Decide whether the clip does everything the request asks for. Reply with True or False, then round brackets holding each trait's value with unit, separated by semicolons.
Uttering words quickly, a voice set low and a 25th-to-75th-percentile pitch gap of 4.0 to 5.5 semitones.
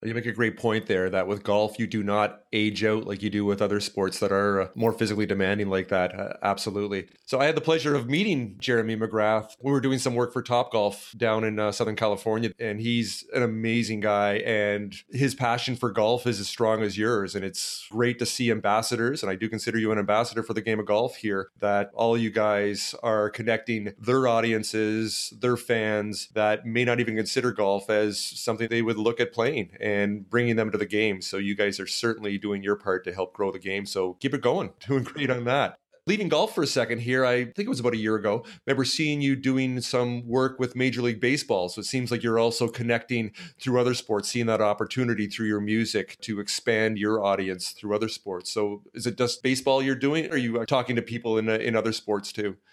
False (230 wpm; 110 Hz; 2.6 semitones)